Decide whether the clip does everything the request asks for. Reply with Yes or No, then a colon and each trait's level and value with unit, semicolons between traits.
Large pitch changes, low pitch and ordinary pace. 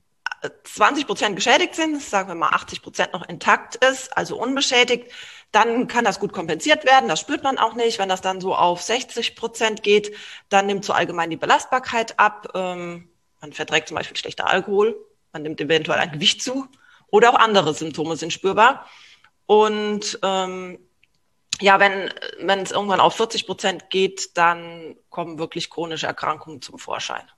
No: wide, 5.7 semitones; high, 195 Hz; average, 165 wpm